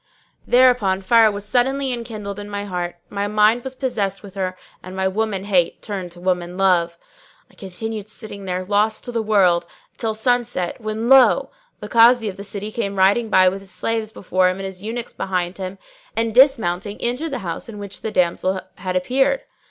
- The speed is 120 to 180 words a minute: No, average, 190 wpm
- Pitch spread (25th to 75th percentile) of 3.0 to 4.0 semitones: Yes, average, 3.4 semitones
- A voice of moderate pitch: No, high, 205 Hz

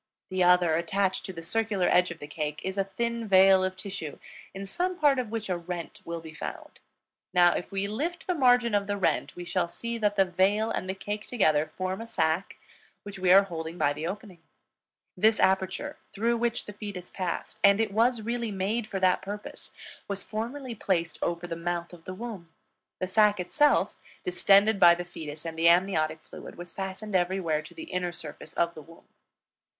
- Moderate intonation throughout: Yes, average, 3.6 semitones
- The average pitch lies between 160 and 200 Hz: Yes, high, 190 Hz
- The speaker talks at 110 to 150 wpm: No, average, 200 wpm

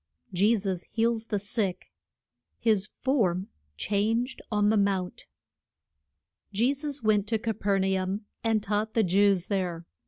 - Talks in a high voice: Yes, high, 205 Hz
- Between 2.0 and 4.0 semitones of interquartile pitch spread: Yes, average, 2.7 semitones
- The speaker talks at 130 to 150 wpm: Yes, slow, 135 wpm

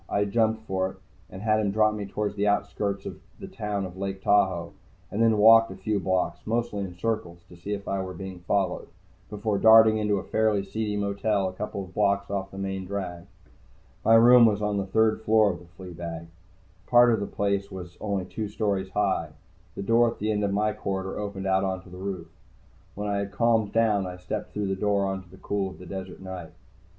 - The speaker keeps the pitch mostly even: Yes, narrow, 2.0 semitones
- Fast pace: Yes, fast, 220 wpm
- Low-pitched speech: Yes, low, 100 Hz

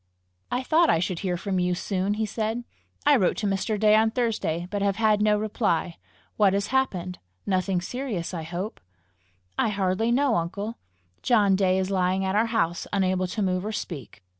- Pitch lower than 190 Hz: No, high, 200 Hz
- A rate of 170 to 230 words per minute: Yes, average, 190 wpm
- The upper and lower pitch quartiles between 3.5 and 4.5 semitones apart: No, average, 3.1 semitones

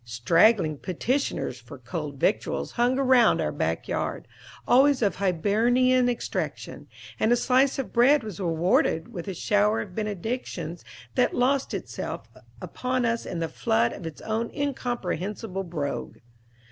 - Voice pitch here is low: No, high, 210 Hz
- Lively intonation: Yes, wide, 6.8 semitones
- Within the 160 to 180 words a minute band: No, average, 140 wpm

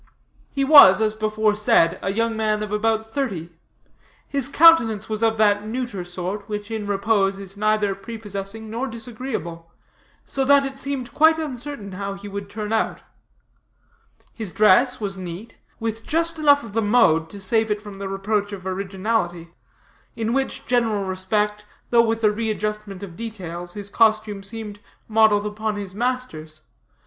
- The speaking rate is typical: Yes, average, 155 wpm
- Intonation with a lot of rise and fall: No, narrow, 2.6 semitones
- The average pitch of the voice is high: Yes, high, 215 Hz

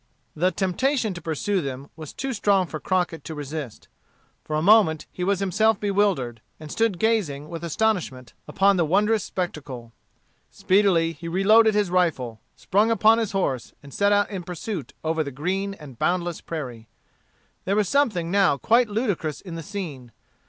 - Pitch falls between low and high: Yes, medium, 180 Hz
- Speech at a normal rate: Yes, average, 165 wpm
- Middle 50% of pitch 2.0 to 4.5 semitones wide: No, average, 4.9 semitones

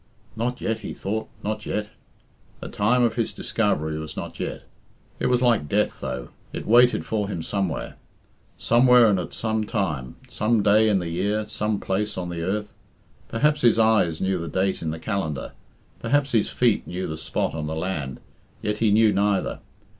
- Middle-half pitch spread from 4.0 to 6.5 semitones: Yes, average, 4.3 semitones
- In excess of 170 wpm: Yes, average, 185 wpm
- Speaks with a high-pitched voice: No, low, 105 Hz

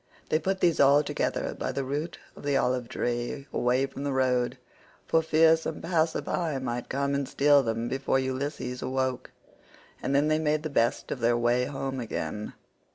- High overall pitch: No, low, 135 Hz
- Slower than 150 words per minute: No, average, 185 wpm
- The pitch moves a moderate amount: Yes, average, 3.0 semitones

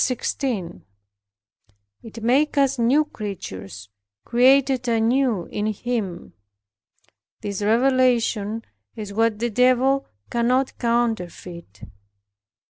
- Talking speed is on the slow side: Yes, slow, 80 wpm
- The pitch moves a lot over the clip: No, average, 3.6 semitones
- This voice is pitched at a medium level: No, high, 235 Hz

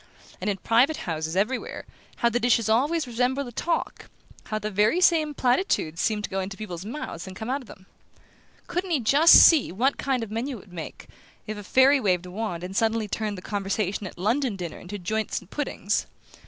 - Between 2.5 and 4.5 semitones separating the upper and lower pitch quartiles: No, average, 5.3 semitones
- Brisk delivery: Yes, fast, 210 wpm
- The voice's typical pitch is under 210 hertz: No, high, 220 Hz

